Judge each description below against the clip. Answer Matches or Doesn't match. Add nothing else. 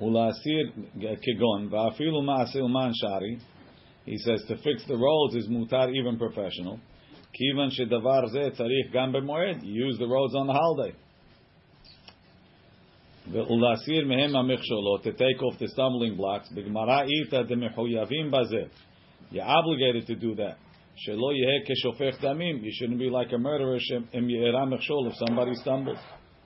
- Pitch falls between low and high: Doesn't match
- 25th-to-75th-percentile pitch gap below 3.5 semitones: Matches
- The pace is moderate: Doesn't match